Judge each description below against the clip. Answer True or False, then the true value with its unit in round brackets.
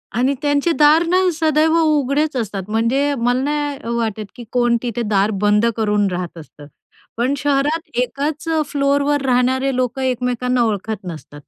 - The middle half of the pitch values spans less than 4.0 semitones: False (4.5 semitones)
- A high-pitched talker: True (255 Hz)